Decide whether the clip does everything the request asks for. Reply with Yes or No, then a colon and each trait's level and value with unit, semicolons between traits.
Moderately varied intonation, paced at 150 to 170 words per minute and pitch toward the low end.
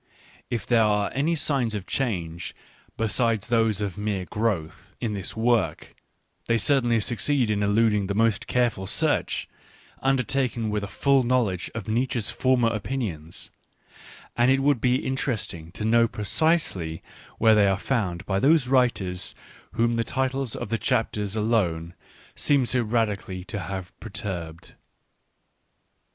No: average, 4.0 semitones; average, 140 wpm; low, 110 Hz